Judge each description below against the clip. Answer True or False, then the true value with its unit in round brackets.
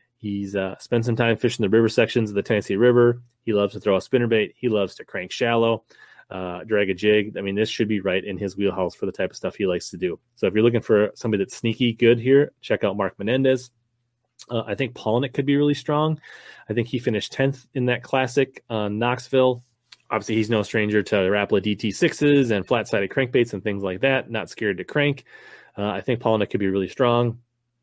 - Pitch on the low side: True (115 Hz)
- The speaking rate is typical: False (230 wpm)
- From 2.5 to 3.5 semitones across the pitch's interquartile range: True (3.0 semitones)